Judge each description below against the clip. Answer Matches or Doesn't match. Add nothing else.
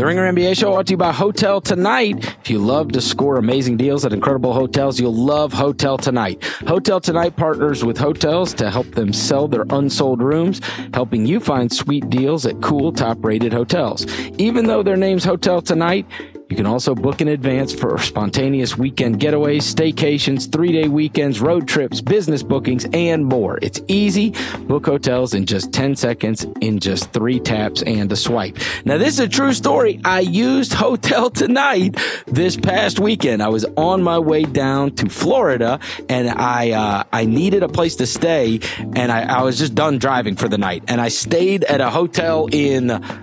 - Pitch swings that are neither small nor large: Doesn't match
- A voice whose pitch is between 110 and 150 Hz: Matches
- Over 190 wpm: Doesn't match